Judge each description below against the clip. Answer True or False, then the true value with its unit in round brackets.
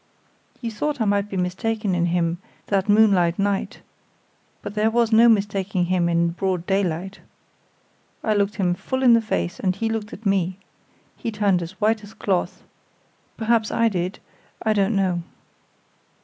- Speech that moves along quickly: False (165 wpm)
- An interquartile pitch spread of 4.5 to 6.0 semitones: False (3.3 semitones)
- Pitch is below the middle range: False (200 Hz)